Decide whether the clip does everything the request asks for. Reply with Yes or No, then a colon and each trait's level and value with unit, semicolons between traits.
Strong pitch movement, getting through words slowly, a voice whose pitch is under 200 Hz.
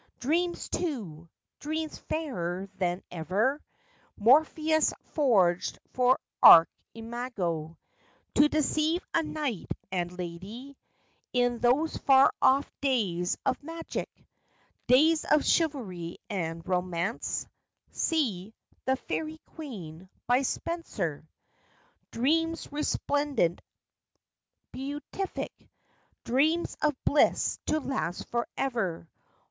No: wide, 8.8 semitones; slow, 90 wpm; very high, 255 Hz